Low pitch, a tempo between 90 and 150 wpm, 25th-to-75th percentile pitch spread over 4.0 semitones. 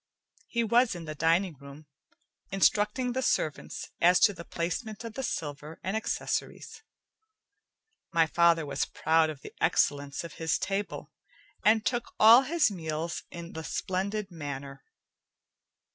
No: medium, 170 Hz; average, 140 wpm; wide, 5.4 semitones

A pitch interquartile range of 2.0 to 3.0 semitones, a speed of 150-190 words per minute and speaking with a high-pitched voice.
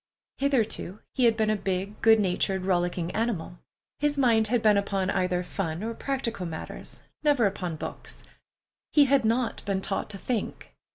No: average, 4.1 semitones; average, 165 wpm; high, 210 Hz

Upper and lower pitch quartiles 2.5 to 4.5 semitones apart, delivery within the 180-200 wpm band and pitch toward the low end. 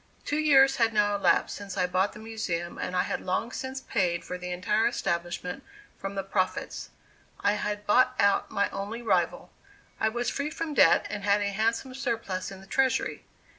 No: average, 4.2 semitones; average, 190 wpm; high, 205 Hz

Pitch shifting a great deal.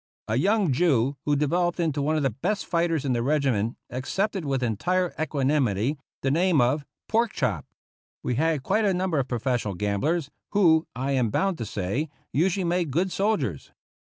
Yes: wide, 5.7 semitones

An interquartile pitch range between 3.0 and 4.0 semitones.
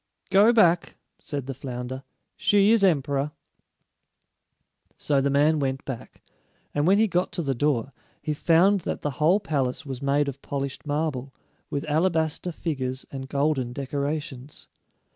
Yes: average, 3.3 semitones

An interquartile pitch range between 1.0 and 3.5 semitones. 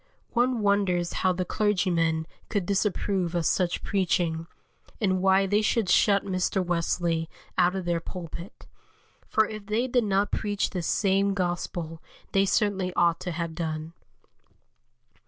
Yes: average, 2.8 semitones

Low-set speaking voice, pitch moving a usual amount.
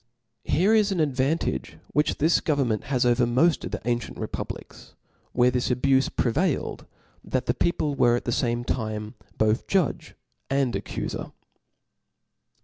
Yes: low, 130 Hz; average, 4.1 semitones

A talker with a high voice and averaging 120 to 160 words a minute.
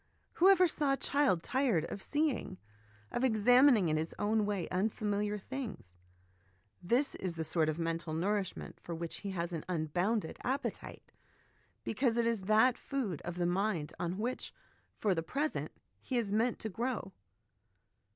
Yes: high, 205 Hz; average, 155 wpm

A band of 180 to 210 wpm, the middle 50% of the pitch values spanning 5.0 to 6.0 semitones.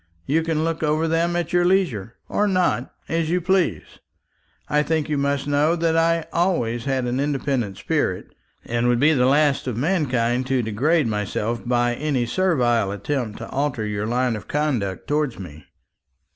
No: average, 170 wpm; wide, 5.4 semitones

